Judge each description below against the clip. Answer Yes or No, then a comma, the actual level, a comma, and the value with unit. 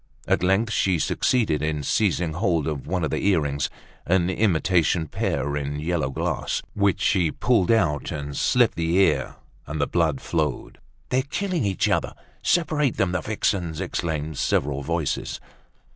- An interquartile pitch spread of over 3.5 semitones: Yes, average, 4.5 semitones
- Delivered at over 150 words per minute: No, average, 145 wpm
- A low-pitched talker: Yes, very low, 85 Hz